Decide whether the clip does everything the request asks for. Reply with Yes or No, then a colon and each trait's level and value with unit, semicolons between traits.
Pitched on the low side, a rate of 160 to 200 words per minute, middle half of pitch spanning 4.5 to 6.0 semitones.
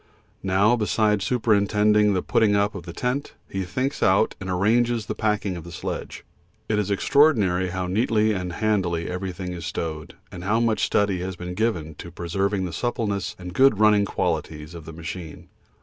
No: low, 100 Hz; average, 180 wpm; average, 3.3 semitones